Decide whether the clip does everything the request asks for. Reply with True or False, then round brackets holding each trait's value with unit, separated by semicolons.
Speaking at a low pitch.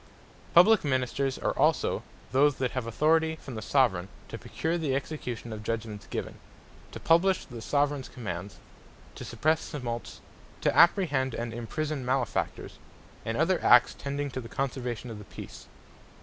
True (130 Hz)